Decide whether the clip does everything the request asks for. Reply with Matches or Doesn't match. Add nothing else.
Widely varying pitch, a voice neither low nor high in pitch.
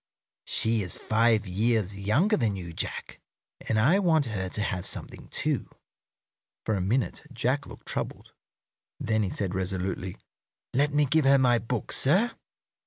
Doesn't match